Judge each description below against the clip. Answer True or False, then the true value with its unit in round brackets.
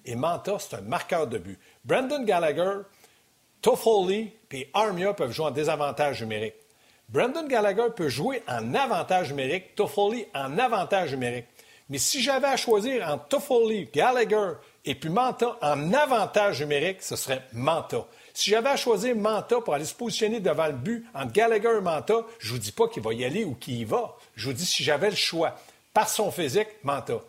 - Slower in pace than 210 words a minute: True (185 wpm)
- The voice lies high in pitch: True (200 Hz)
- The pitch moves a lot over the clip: True (7.7 semitones)